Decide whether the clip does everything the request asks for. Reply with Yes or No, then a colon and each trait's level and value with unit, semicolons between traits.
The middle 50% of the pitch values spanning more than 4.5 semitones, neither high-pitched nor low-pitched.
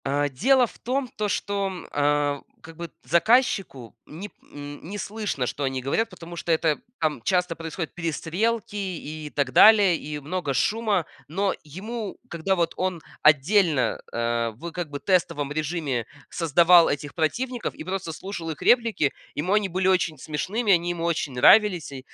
Yes: average, 5.1 semitones; medium, 170 Hz